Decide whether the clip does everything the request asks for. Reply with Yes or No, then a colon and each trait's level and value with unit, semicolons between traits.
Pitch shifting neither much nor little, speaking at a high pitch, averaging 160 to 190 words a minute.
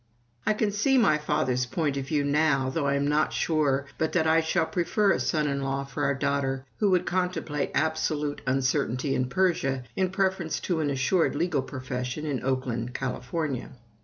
No: average, 3.5 semitones; medium, 145 Hz; average, 185 wpm